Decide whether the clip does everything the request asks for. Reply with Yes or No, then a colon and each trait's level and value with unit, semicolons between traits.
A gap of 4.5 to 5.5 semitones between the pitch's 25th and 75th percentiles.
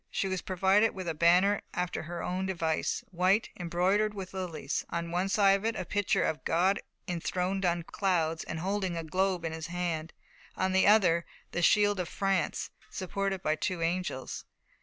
No: narrow, 2.4 semitones